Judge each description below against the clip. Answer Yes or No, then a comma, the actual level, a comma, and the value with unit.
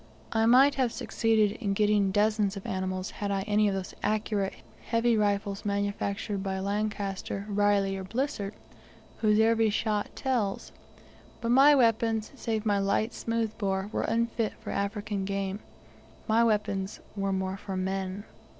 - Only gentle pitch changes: Yes, narrow, 2.2 semitones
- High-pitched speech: Yes, high, 205 Hz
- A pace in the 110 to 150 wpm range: Yes, average, 145 wpm